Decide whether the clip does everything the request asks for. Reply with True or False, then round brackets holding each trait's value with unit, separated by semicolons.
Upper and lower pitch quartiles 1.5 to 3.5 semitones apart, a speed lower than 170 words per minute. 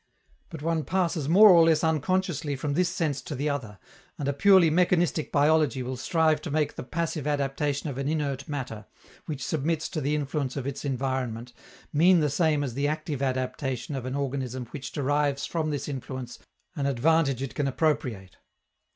False (3.1 semitones; 180 wpm)